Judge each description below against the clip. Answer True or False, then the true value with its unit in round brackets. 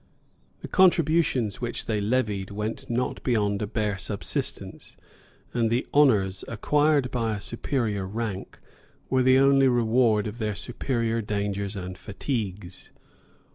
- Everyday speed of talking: False (130 wpm)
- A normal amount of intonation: True (3.9 semitones)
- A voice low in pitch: True (115 Hz)